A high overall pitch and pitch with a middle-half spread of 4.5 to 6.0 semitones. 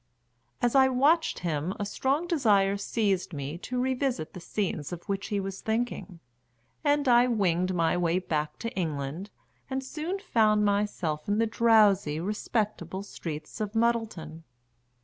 Yes: high, 205 Hz; wide, 5.6 semitones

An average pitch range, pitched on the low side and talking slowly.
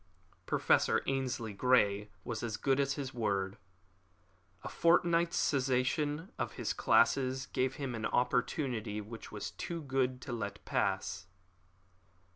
Yes: average, 3.9 semitones; low, 130 Hz; slow, 125 wpm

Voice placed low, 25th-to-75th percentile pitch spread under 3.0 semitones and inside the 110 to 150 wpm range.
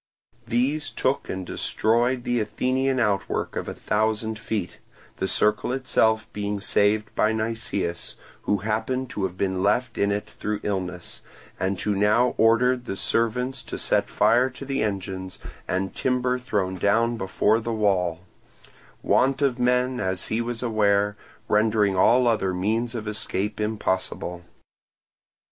No: low, 110 Hz; average, 3.4 semitones; average, 145 wpm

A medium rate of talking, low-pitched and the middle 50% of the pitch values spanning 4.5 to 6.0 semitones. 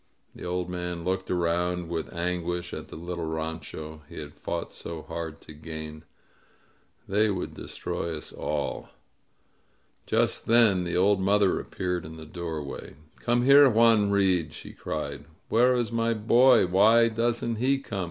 Yes: average, 150 wpm; very low, 90 Hz; average, 5.2 semitones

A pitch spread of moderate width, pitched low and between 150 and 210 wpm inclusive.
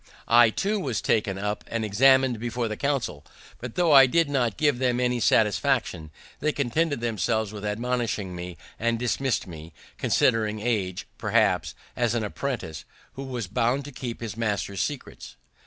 Yes: average, 4.0 semitones; low, 115 Hz; average, 160 wpm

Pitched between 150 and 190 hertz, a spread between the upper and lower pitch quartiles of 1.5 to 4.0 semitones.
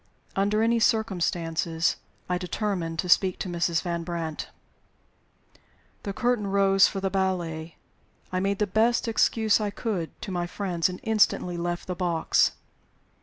Yes: medium, 185 Hz; average, 3.2 semitones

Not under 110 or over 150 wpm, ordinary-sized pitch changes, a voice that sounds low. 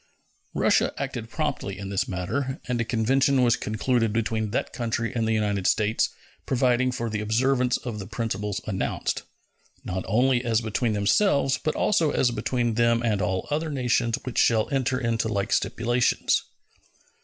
No: average, 160 wpm; average, 3.0 semitones; low, 115 Hz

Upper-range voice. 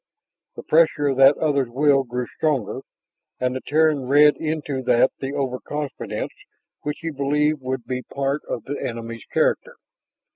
No: medium, 140 Hz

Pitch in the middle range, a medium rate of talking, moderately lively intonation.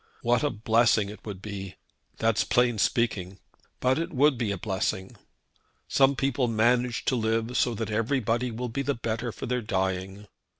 No: low, 115 Hz; average, 170 wpm; average, 3.1 semitones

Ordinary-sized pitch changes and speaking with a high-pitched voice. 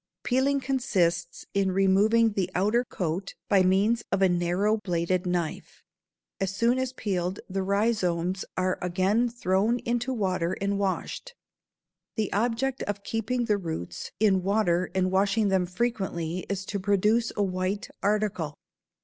Yes: average, 3.3 semitones; high, 195 Hz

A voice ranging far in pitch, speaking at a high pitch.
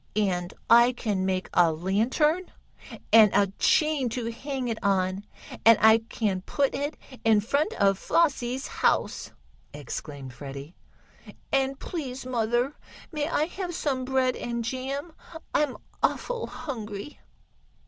Yes: wide, 5.7 semitones; high, 240 Hz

